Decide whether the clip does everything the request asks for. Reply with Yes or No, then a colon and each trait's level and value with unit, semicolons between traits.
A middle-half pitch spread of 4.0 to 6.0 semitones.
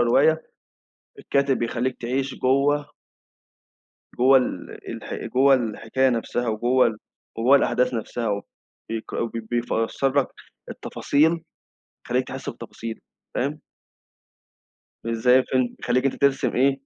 No: average, 2.7 semitones